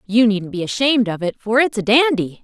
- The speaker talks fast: Yes, fast, 245 wpm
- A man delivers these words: No, female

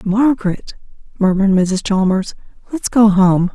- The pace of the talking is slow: Yes, slow, 120 wpm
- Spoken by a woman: Yes, female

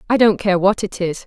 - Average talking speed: No, fast, 285 wpm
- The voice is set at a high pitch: Yes, high, 195 Hz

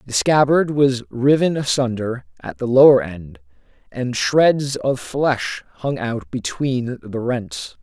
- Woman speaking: No, male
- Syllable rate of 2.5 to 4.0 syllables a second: Yes, 3.6 syllables/s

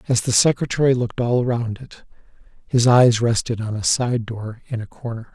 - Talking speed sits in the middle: Yes, average, 190 wpm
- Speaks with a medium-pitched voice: No, low, 120 Hz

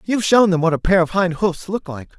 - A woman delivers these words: No, male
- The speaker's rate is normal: No, fast, 300 wpm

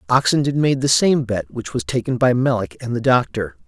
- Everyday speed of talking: No, fast, 210 wpm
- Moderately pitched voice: No, low, 125 Hz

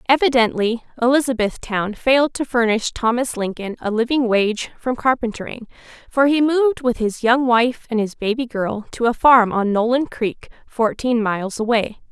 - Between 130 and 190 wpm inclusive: Yes, average, 160 wpm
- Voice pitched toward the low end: No, high, 235 Hz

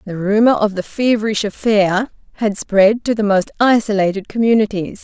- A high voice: Yes, high, 210 Hz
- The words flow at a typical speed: Yes, average, 155 wpm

